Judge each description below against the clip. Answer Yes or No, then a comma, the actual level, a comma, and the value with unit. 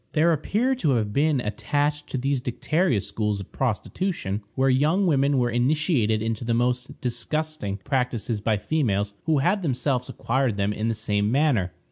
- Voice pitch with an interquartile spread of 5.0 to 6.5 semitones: Yes, wide, 5.5 semitones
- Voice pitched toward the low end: Yes, low, 125 Hz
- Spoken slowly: No, average, 165 wpm